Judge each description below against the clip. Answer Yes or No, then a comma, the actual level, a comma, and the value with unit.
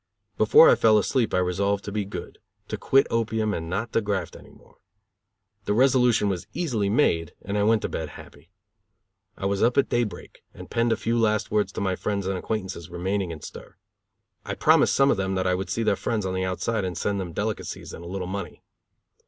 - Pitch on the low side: Yes, low, 100 Hz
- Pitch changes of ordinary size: Yes, average, 3.2 semitones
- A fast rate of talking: Yes, fast, 220 wpm